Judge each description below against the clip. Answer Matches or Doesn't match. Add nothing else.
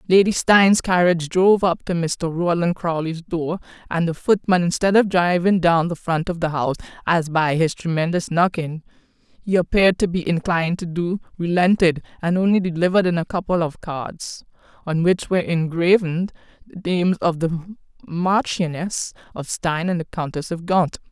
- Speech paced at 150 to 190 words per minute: Matches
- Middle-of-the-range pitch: Matches